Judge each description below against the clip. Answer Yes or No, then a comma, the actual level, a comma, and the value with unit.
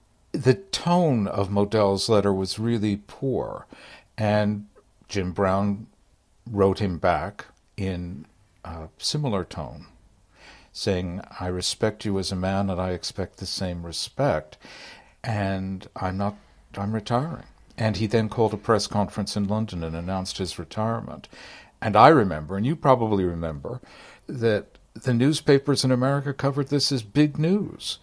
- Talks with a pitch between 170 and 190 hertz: No, low, 100 Hz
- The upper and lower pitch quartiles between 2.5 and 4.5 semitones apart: Yes, average, 3.6 semitones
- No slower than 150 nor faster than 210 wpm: No, average, 140 wpm